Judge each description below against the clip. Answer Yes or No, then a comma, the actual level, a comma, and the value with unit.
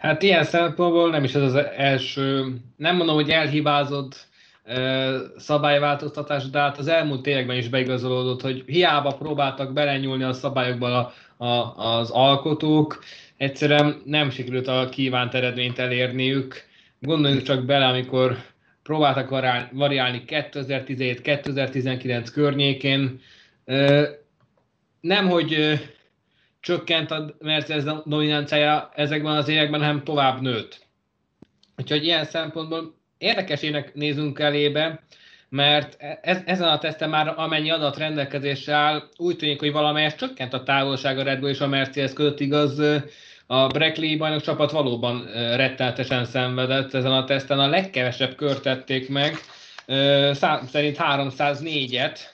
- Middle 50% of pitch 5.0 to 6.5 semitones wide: No, narrow, 2.4 semitones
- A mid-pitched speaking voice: Yes, medium, 145 Hz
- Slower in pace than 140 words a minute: Yes, average, 120 wpm